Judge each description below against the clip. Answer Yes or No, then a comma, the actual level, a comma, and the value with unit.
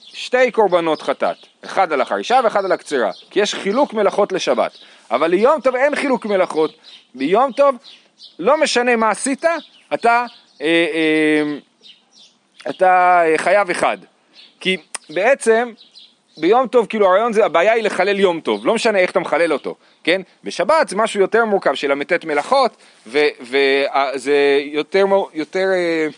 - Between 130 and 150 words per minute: Yes, average, 145 wpm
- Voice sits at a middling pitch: No, high, 195 Hz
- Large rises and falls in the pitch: Yes, wide, 7.1 semitones